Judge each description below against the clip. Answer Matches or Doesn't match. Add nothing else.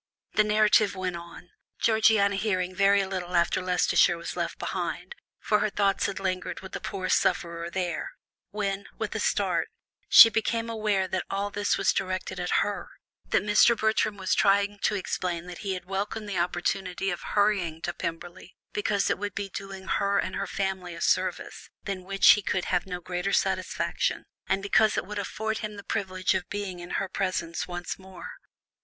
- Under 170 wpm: Doesn't match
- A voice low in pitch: Doesn't match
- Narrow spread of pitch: Matches